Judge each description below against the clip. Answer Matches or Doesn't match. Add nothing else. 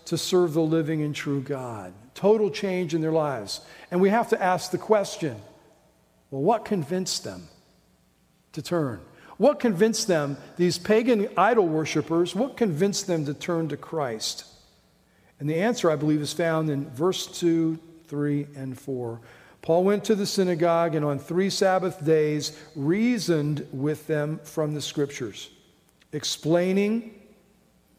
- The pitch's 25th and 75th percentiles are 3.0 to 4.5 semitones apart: Matches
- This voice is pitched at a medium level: Matches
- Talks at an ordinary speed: Matches